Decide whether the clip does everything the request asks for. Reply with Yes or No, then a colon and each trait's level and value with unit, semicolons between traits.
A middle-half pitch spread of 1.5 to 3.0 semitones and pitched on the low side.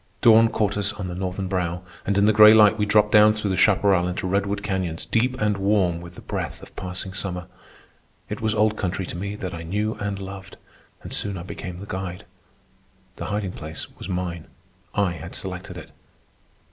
Yes: narrow, 2.5 semitones; very low, 95 Hz